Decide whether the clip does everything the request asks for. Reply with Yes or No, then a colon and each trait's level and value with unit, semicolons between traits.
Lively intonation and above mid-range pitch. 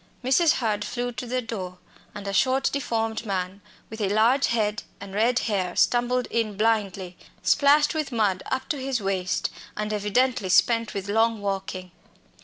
No: average, 3.8 semitones; high, 220 Hz